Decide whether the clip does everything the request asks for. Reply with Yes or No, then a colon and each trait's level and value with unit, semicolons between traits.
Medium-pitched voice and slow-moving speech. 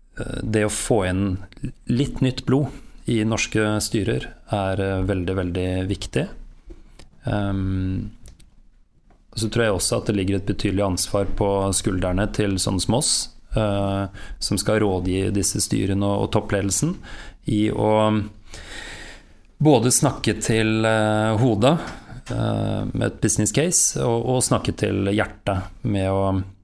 No: low, 105 Hz; slow, 120 wpm